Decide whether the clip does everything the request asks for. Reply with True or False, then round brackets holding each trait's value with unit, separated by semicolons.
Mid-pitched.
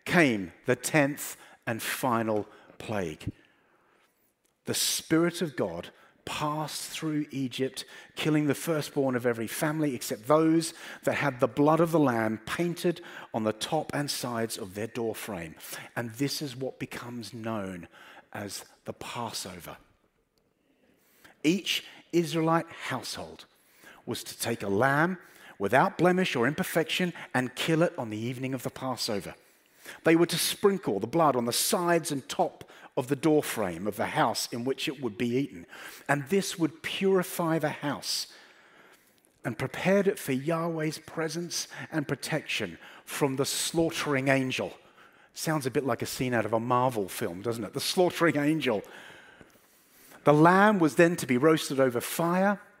True (145 Hz)